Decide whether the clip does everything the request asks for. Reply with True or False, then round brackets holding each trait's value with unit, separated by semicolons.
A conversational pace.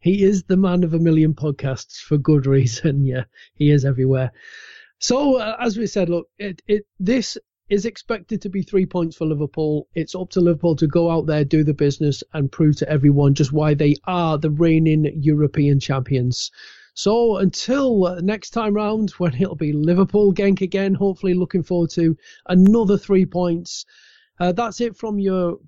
True (180 wpm)